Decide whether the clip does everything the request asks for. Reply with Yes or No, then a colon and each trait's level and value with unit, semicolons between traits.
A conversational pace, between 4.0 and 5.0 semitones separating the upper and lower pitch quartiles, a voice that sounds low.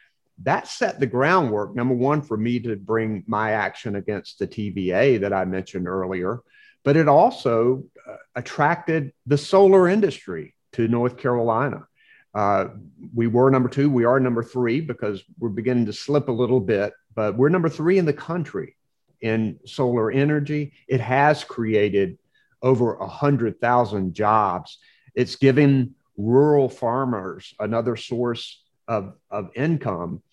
Yes: average, 145 wpm; average, 4.4 semitones; low, 125 Hz